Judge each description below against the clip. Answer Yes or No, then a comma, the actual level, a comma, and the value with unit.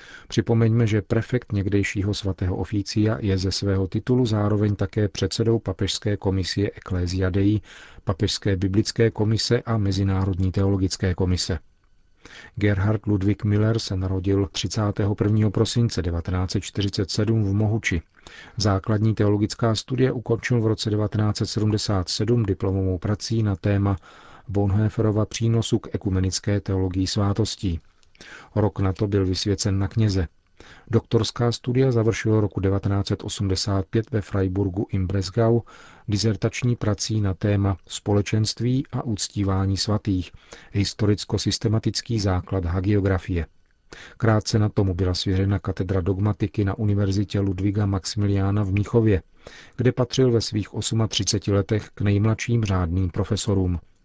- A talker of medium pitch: No, low, 105 Hz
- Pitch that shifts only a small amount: Yes, narrow, 2.3 semitones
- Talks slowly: Yes, slow, 110 wpm